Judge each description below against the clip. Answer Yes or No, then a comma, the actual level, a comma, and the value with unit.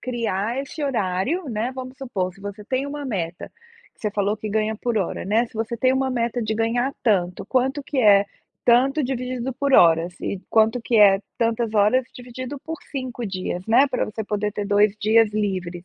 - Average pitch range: Yes, average, 3.9 semitones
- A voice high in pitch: Yes, high, 225 Hz